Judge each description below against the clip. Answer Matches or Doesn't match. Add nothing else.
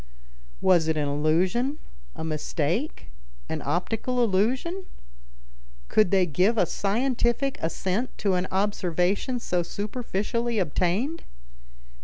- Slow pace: Matches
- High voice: Matches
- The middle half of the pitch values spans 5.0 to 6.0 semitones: Matches